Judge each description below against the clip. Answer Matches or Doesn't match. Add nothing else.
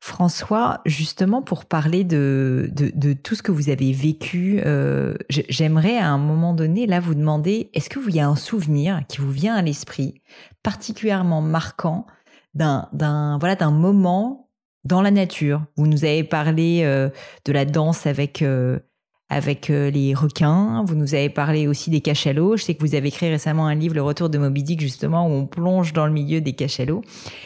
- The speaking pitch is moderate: Matches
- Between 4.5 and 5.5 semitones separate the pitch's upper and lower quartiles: Doesn't match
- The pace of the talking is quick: Doesn't match